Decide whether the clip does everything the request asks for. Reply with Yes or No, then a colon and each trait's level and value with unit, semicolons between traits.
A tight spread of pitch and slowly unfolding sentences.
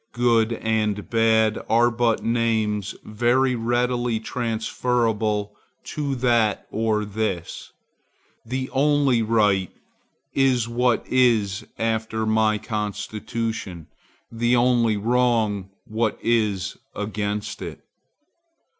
Yes: narrow, 2.2 semitones; slow, 95 wpm